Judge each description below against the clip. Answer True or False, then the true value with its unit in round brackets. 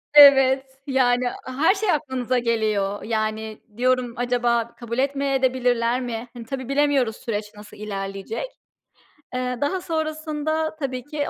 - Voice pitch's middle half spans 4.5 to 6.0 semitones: False (3.5 semitones)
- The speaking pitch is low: False (255 Hz)